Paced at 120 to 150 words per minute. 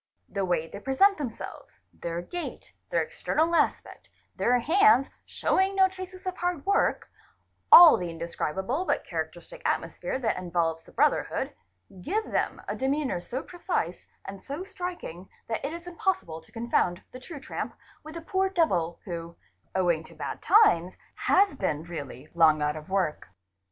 No: average, 160 wpm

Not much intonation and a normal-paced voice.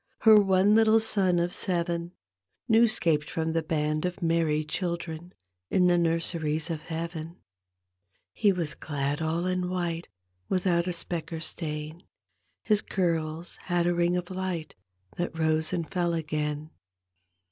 Yes: narrow, 2.3 semitones; average, 145 wpm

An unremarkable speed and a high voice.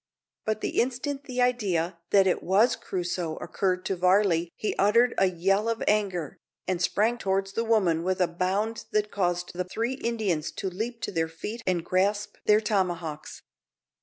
Yes: average, 170 wpm; high, 195 Hz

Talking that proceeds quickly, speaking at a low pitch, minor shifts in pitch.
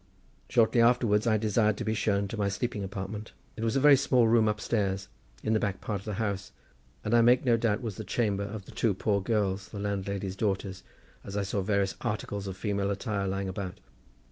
Yes: fast, 215 wpm; low, 105 Hz; narrow, 2.1 semitones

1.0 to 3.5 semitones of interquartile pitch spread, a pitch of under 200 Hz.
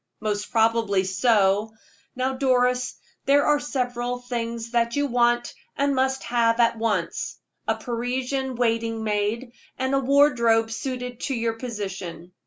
No: narrow, 2.4 semitones; high, 240 Hz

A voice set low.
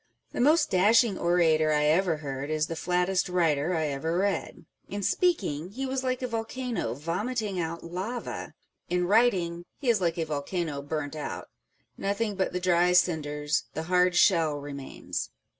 No: medium, 180 Hz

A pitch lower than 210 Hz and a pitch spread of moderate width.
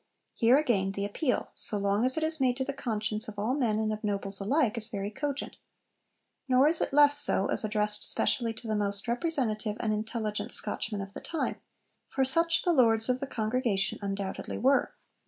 No: high, 225 Hz; average, 4.1 semitones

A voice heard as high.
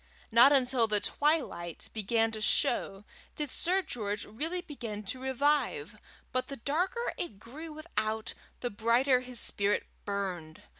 Yes: high, 245 Hz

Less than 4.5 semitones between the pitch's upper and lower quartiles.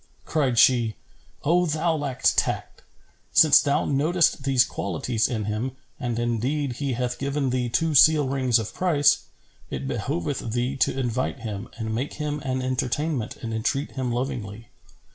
Yes: average, 3.6 semitones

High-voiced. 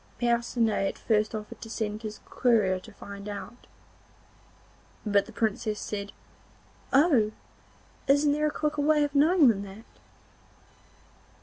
Yes: high, 225 Hz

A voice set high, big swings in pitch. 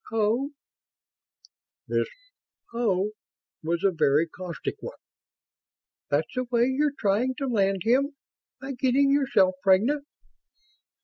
Yes: high, 230 Hz; wide, 6.1 semitones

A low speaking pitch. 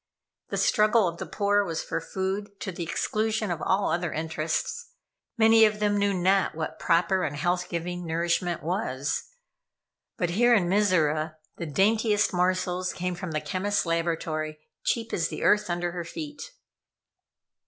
No: medium, 180 Hz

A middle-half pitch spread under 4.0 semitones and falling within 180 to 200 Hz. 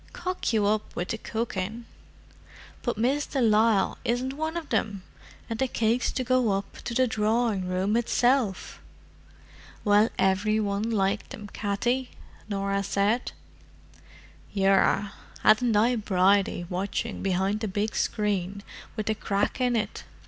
No: average, 3.0 semitones; high, 215 Hz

